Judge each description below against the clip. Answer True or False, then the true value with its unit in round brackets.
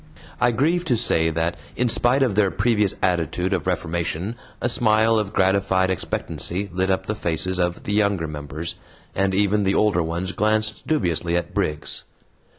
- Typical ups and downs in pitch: True (3.7 semitones)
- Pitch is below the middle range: True (95 Hz)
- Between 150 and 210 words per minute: True (165 wpm)